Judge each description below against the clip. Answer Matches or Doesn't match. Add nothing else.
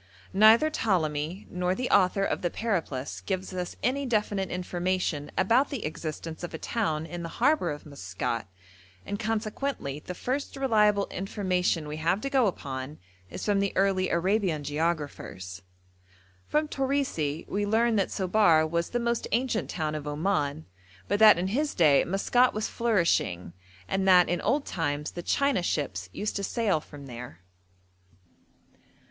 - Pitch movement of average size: Doesn't match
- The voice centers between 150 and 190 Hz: Matches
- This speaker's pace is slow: Doesn't match